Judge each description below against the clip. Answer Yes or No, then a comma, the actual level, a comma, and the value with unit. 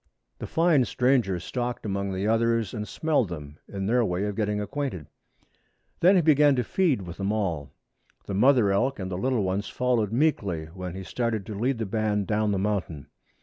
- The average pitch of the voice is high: No, low, 105 Hz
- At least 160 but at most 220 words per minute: Yes, average, 190 wpm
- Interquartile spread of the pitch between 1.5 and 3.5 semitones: No, average, 4.5 semitones